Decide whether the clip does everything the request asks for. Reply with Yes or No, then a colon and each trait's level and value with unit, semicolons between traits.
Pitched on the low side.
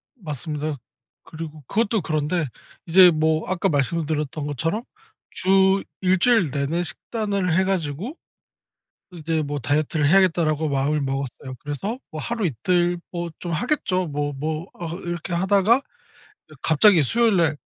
No: medium, 165 Hz